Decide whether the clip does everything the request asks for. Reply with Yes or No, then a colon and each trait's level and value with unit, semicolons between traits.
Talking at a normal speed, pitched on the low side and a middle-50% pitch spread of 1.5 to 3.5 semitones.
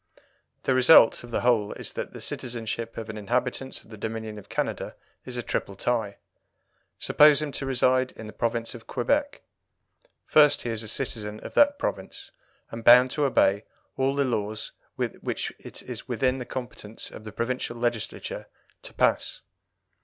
Yes: average, 170 wpm; low, 120 Hz; average, 2.9 semitones